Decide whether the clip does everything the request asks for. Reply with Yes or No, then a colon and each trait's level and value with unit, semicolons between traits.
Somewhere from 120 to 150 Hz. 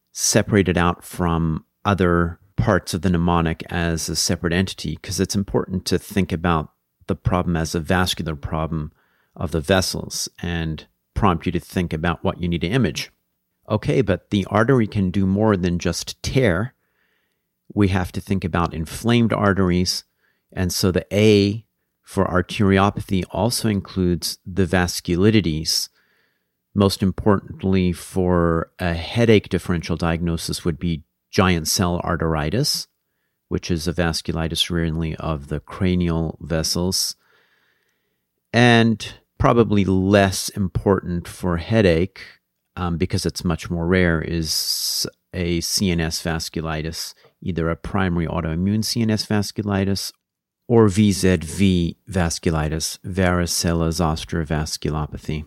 No: very low, 90 Hz